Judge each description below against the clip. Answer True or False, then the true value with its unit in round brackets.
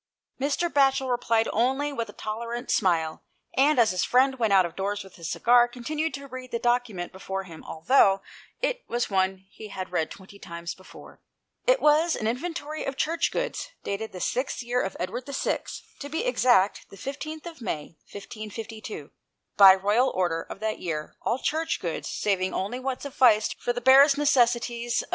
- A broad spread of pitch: True (5.9 semitones)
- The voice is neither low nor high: False (235 Hz)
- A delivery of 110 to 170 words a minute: False (190 wpm)